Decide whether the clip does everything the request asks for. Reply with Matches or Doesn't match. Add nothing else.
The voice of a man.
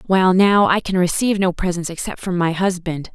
Doesn't match